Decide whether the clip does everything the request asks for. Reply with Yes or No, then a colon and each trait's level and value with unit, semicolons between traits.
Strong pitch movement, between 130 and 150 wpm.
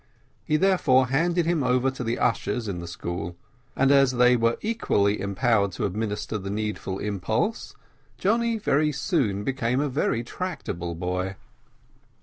Yes: wide, 6.5 semitones; average, 145 wpm